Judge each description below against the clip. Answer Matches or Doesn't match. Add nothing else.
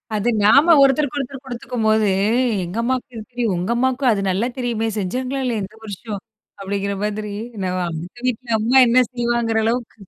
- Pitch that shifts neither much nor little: Matches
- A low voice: Doesn't match